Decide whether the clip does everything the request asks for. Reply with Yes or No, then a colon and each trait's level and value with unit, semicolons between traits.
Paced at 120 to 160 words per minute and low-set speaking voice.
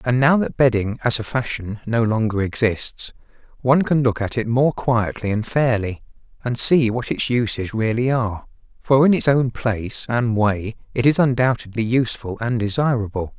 No: average, 175 wpm; low, 120 Hz